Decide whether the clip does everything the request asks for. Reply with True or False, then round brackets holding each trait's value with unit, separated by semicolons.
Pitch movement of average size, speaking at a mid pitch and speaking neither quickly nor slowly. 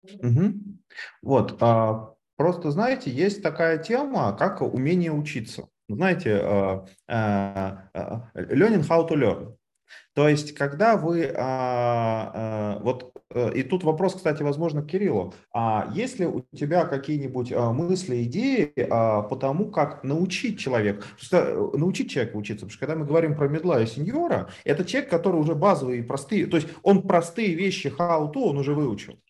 False (7.0 semitones; 150 Hz; 150 wpm)